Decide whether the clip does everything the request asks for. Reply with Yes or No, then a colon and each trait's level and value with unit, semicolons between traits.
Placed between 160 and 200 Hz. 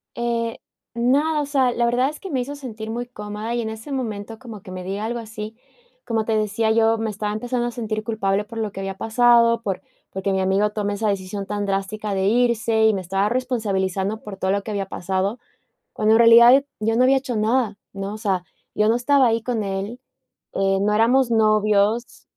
No: high, 220 Hz